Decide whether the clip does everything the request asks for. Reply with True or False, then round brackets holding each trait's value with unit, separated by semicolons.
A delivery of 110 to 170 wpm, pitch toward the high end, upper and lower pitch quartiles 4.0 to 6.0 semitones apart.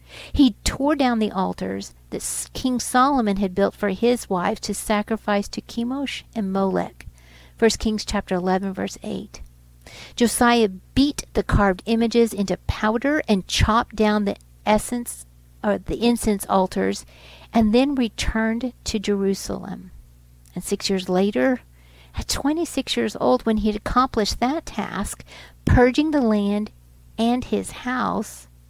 True (140 wpm; 210 Hz; 4.5 semitones)